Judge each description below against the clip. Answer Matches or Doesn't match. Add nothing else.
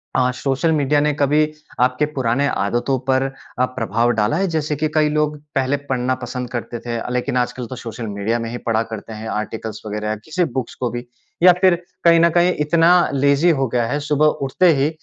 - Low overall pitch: Matches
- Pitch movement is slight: Doesn't match